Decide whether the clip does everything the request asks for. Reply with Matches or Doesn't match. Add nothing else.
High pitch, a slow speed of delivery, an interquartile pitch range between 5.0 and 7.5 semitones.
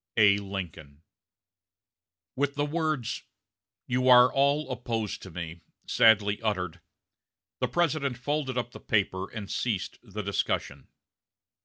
Doesn't match